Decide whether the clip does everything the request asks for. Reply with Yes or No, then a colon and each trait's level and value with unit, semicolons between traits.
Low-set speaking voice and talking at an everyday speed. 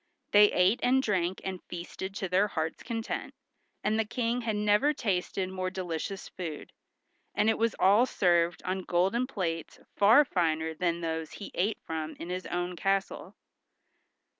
No: high, 190 Hz; average, 160 wpm